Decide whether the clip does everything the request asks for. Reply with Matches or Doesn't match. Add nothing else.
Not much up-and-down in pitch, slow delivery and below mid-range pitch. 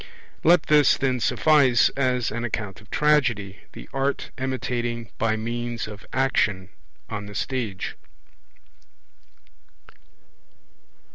Doesn't match